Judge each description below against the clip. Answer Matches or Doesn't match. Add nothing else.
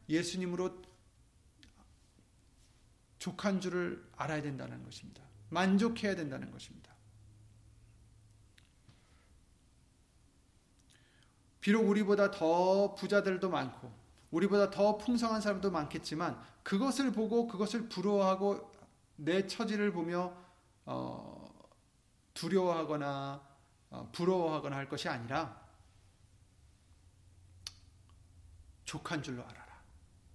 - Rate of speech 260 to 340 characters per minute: Doesn't match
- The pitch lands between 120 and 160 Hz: Matches